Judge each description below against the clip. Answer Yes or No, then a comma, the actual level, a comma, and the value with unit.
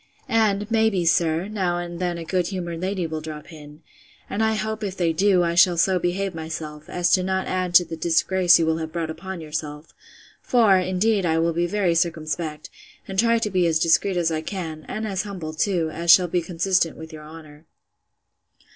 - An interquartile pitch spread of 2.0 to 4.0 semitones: Yes, average, 2.9 semitones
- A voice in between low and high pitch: Yes, medium, 175 Hz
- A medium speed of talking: No, fast, 210 wpm